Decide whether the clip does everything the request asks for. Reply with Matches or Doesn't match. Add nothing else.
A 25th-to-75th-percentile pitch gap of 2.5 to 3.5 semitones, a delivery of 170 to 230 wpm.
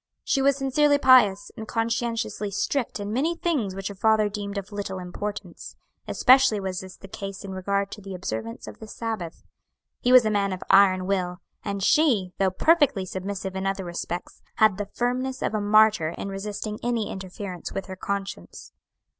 Matches